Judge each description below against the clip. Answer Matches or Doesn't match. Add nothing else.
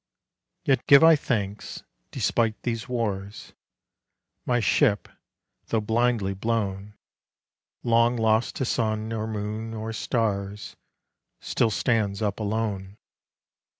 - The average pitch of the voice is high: Doesn't match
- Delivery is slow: Matches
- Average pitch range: Doesn't match